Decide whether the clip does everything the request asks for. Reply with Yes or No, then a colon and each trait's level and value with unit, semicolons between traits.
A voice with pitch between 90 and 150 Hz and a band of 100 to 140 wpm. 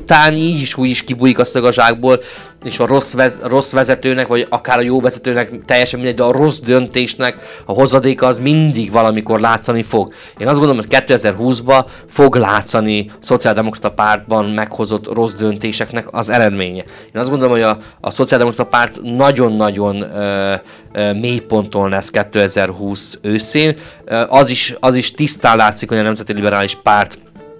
No: low, 120 Hz; fast, 155 wpm